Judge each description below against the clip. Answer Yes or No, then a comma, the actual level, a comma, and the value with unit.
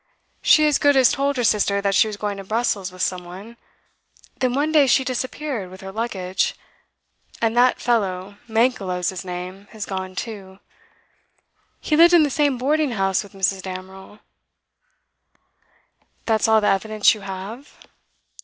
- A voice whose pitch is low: No, high, 210 Hz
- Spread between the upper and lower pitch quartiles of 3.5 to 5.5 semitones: Yes, average, 4.8 semitones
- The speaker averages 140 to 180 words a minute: Yes, average, 165 wpm